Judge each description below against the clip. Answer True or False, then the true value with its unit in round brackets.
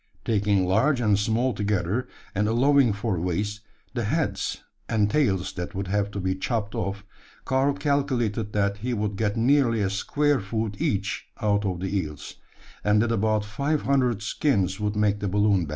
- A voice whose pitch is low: True (105 Hz)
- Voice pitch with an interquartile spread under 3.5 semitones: True (3.1 semitones)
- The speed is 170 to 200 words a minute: True (175 wpm)